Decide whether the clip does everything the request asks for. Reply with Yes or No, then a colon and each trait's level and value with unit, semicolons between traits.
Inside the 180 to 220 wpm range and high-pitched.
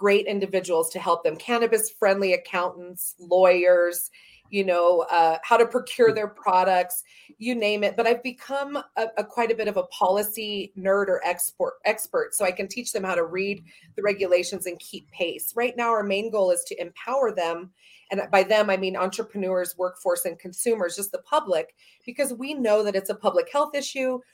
Yes: average, 190 wpm; high, 200 Hz